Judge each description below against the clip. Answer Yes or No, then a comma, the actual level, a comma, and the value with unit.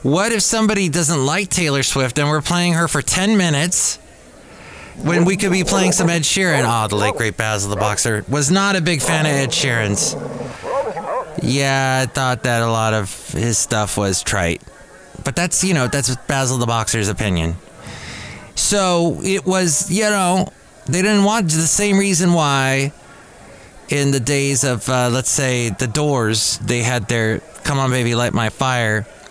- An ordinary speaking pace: Yes, average, 180 wpm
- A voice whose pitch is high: No, medium, 140 Hz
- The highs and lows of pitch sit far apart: Yes, wide, 6.8 semitones